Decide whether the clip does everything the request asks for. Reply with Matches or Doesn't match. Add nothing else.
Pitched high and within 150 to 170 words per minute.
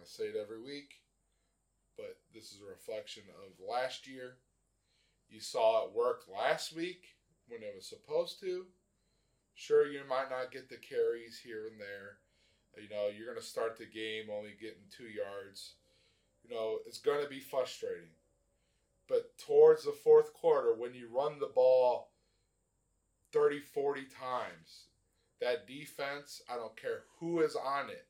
Doesn't match